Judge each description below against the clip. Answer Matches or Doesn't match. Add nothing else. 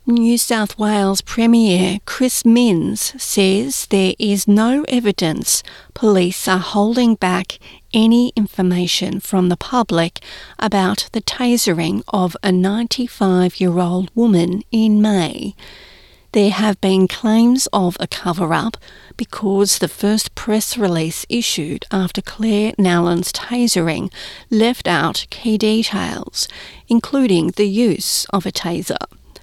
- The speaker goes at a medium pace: Doesn't match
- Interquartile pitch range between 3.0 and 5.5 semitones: Matches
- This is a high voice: Matches